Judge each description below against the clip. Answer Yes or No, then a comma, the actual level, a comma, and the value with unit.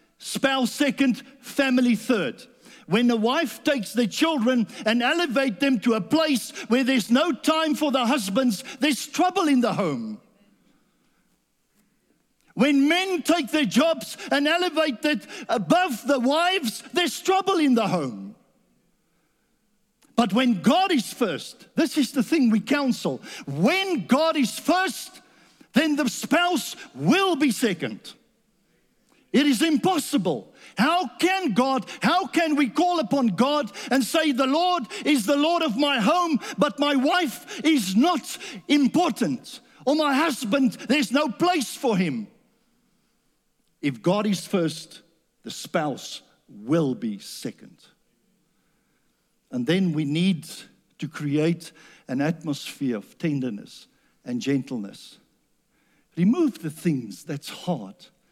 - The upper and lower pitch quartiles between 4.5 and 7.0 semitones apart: Yes, average, 5.3 semitones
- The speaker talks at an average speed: No, slow, 130 wpm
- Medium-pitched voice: No, very high, 255 Hz